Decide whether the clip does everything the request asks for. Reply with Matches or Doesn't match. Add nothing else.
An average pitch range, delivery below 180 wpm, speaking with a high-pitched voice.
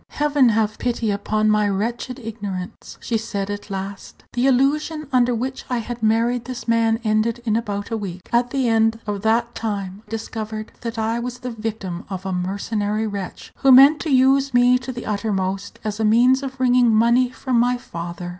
Doesn't match